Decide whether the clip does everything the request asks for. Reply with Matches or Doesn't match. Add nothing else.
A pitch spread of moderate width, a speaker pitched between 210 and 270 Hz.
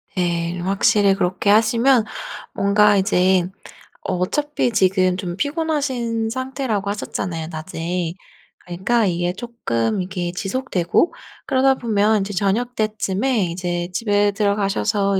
Doesn't match